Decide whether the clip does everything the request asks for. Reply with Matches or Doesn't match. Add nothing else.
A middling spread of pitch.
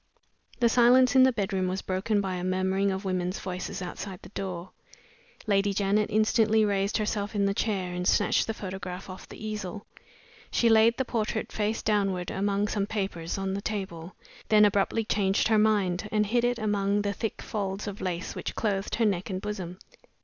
Doesn't match